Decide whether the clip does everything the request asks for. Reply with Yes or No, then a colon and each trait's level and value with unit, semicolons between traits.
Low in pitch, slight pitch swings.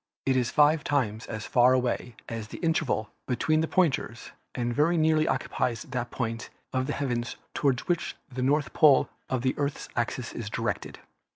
No: low, 130 Hz; average, 3.7 semitones